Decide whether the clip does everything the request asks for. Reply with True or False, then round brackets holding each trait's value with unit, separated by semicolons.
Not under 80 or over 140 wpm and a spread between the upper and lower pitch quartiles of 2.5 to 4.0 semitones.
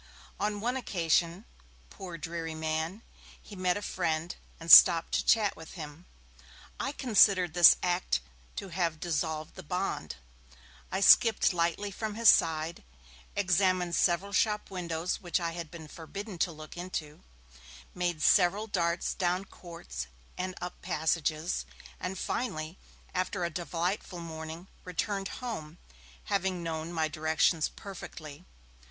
True (135 wpm; 2.9 semitones)